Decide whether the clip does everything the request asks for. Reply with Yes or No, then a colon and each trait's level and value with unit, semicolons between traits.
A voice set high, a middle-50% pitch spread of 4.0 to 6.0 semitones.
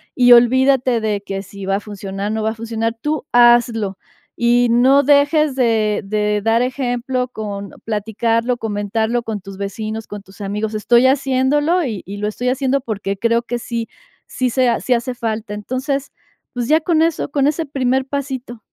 No: high, 235 Hz; average, 3.5 semitones